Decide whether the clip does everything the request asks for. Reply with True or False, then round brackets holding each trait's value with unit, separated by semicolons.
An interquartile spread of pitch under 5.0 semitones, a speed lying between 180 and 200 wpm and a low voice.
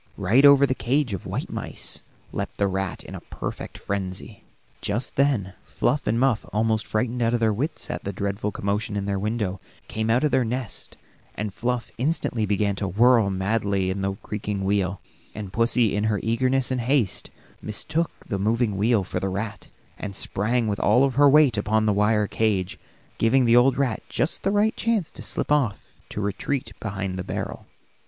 True (3.8 semitones; 190 wpm; 110 Hz)